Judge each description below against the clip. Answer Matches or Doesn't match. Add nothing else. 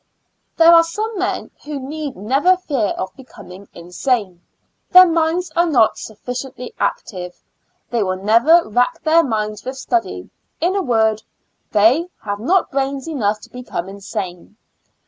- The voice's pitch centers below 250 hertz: Doesn't match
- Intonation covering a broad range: Matches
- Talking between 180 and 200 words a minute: Doesn't match